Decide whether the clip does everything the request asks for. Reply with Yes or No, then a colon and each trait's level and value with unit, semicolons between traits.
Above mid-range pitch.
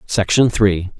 No: low, 100 Hz